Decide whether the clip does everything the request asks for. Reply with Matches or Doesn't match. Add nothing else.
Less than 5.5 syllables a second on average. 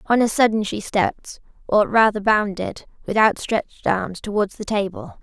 Matches